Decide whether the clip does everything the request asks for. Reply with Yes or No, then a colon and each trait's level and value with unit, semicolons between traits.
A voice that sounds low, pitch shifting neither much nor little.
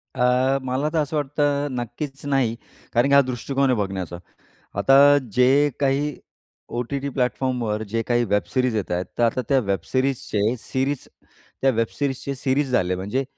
Yes: low, 130 Hz; average, 3.1 semitones